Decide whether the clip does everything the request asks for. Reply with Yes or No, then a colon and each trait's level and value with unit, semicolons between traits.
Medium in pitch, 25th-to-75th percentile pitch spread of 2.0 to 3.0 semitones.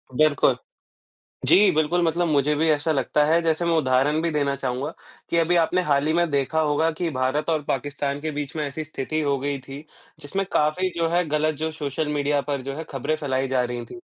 Yes: medium, 150 Hz; narrow, 2.4 semitones